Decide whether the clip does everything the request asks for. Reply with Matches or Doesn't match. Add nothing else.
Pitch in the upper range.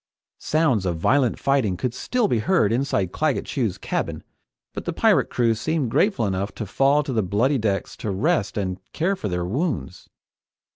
Doesn't match